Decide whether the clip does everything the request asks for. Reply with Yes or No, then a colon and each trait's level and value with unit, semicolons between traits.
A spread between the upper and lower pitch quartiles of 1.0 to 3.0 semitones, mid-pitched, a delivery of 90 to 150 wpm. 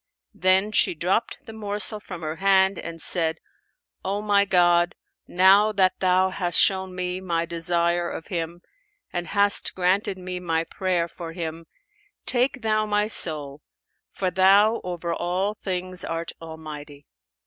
Yes: average, 2.7 semitones; medium, 180 Hz; average, 145 wpm